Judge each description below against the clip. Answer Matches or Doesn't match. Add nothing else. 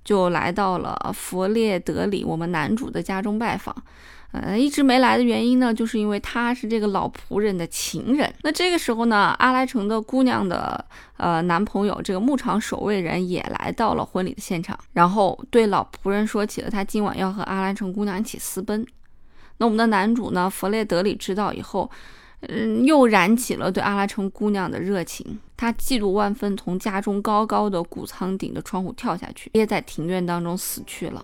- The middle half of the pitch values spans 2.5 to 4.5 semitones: Matches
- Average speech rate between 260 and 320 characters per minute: Matches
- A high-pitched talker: Matches